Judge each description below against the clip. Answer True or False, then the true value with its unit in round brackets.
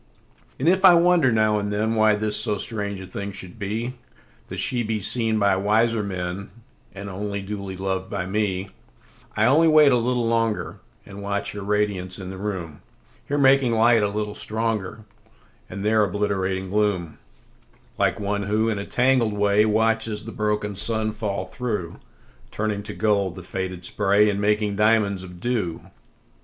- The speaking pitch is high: False (105 Hz)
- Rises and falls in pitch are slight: True (2.2 semitones)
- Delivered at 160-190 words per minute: False (145 wpm)